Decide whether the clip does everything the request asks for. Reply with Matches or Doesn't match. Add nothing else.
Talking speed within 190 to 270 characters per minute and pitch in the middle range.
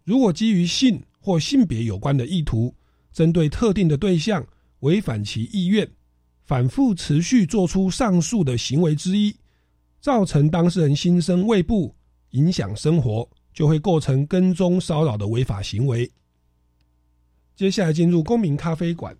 Matches